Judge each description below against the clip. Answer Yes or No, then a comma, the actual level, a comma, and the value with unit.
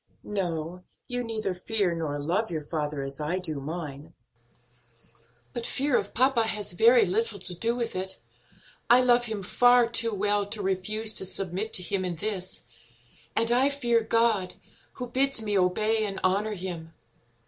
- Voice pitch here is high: Yes, high, 205 Hz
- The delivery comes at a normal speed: Yes, average, 165 wpm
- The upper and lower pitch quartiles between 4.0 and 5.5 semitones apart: Yes, average, 4.3 semitones